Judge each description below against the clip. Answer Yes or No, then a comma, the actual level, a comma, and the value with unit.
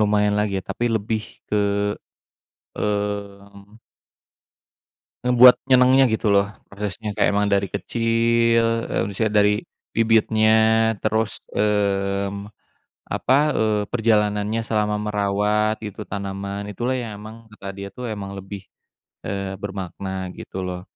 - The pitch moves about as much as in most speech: No, narrow, 1.9 semitones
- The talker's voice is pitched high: No, low, 105 Hz